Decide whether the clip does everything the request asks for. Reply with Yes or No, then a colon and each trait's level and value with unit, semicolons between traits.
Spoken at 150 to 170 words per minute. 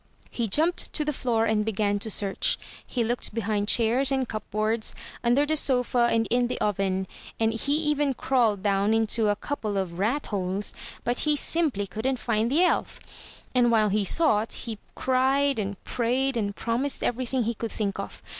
No: average, 185 wpm